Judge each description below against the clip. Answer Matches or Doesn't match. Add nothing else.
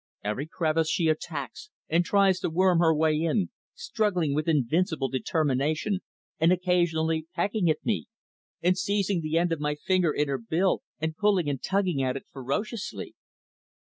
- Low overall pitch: Doesn't match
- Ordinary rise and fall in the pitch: Matches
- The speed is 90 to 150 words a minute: Doesn't match